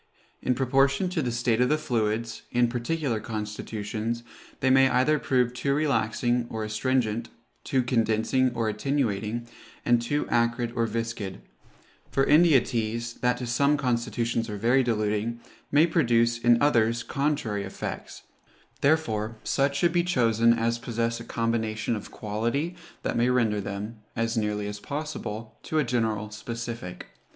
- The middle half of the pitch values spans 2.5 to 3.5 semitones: Yes, average, 2.9 semitones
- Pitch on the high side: No, low, 115 Hz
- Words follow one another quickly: No, average, 145 wpm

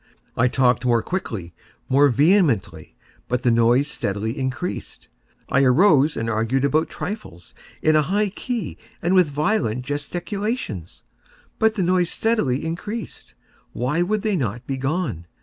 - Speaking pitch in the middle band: Yes, medium, 145 Hz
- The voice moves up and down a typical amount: No, wide, 7.1 semitones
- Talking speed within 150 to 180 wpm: No, slow, 135 wpm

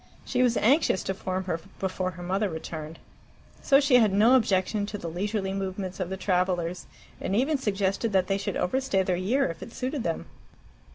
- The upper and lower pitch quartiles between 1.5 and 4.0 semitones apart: Yes, average, 3.6 semitones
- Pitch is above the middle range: Yes, high, 195 Hz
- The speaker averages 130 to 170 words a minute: No, average, 190 wpm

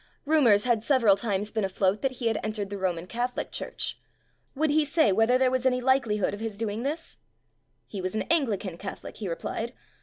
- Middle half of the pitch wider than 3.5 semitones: Yes, average, 4.3 semitones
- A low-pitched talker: No, high, 225 Hz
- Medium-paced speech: No, fast, 210 wpm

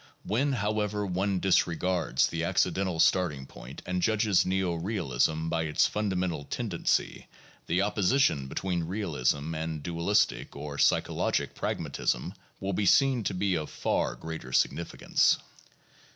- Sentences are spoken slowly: Yes, slow, 130 wpm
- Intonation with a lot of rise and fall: No, average, 3.9 semitones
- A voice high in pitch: No, very low, 90 Hz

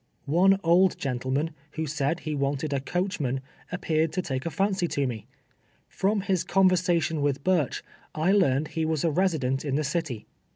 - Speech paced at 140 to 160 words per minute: No, average, 180 wpm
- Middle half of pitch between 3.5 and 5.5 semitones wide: Yes, average, 4.5 semitones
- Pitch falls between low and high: Yes, medium, 160 Hz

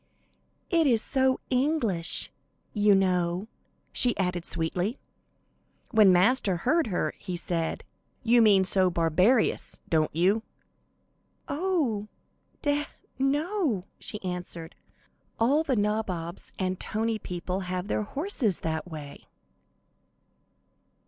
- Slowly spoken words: Yes, slow, 110 wpm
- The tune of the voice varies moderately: No, wide, 6.0 semitones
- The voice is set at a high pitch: Yes, high, 205 Hz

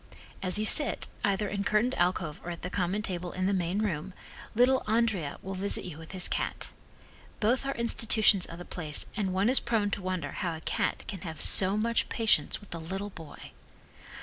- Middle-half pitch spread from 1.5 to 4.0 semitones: Yes, average, 3.3 semitones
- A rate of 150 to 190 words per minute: No, fast, 205 wpm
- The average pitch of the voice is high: Yes, high, 195 Hz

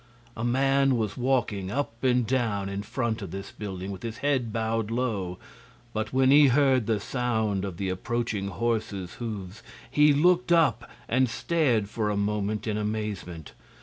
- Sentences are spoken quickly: No, average, 160 wpm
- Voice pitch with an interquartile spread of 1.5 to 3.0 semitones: No, average, 4.2 semitones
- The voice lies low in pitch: Yes, low, 110 Hz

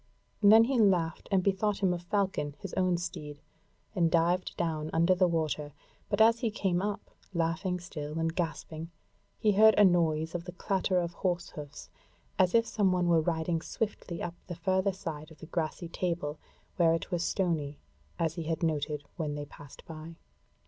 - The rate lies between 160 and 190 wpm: Yes, average, 185 wpm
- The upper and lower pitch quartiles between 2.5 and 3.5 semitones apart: Yes, average, 2.8 semitones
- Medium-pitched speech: Yes, medium, 170 Hz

